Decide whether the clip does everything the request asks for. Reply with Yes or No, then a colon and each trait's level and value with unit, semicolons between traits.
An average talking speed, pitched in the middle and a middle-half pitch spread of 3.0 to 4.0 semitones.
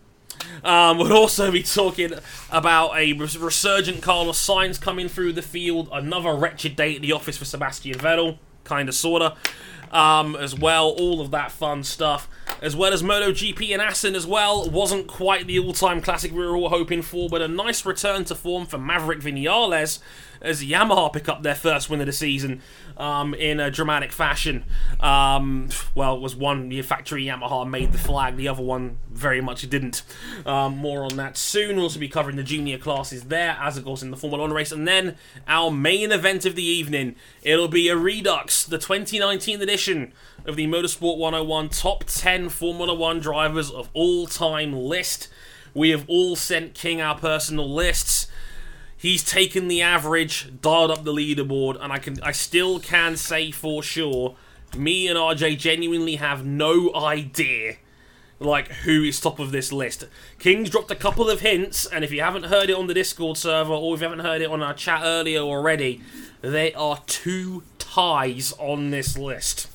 Yes: average, 185 wpm; medium, 160 Hz; average, 3.4 semitones